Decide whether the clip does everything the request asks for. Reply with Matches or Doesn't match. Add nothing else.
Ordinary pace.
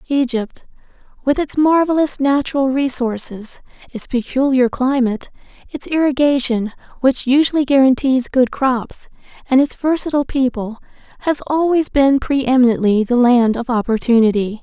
Doesn't match